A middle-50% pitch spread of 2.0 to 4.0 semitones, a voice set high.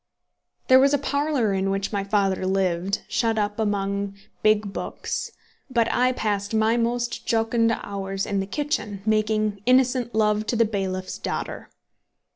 Yes: average, 2.9 semitones; high, 215 Hz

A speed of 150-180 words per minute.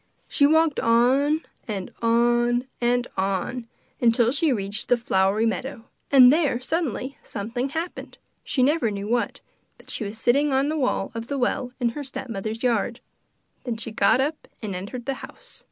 Yes: average, 170 wpm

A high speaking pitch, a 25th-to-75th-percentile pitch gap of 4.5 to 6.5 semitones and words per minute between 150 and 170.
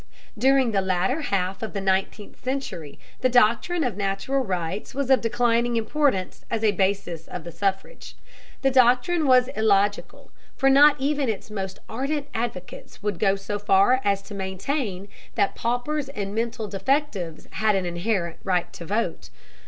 Yes: high, 215 Hz; average, 5.1 semitones; average, 160 wpm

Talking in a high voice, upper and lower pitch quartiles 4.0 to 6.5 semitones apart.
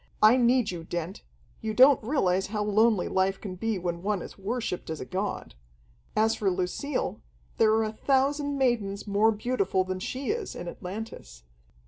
Yes: high, 210 Hz; average, 4.4 semitones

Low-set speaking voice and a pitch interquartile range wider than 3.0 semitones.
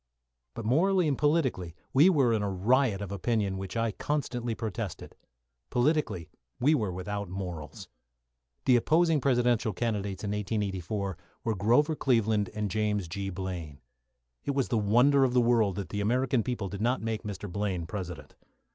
Yes: low, 110 Hz; average, 4.4 semitones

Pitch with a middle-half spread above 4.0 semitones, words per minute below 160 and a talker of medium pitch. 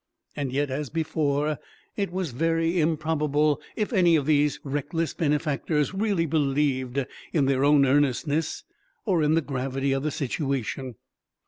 No: average, 2.8 semitones; average, 140 wpm; medium, 150 Hz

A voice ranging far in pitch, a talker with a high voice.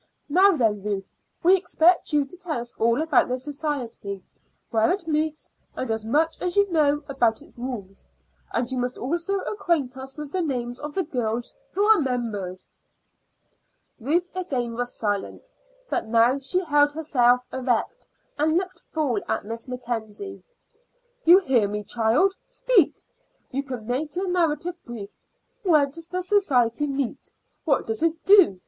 Yes: wide, 5.9 semitones; very high, 275 Hz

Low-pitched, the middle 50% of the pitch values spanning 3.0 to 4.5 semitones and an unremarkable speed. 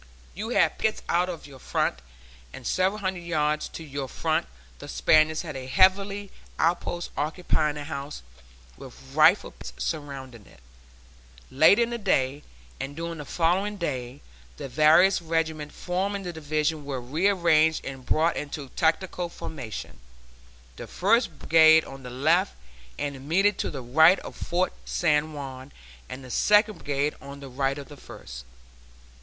No: medium, 155 Hz; average, 4.2 semitones; average, 155 wpm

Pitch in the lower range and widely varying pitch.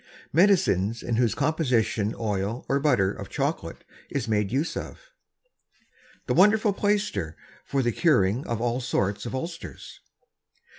Yes: low, 120 Hz; wide, 7.2 semitones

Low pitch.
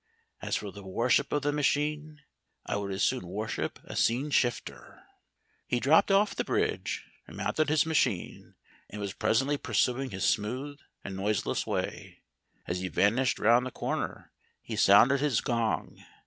Yes: low, 120 Hz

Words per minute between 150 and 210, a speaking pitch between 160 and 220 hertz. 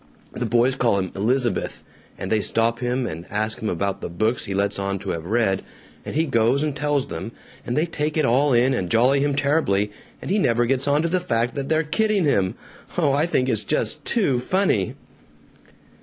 No: average, 200 wpm; low, 125 Hz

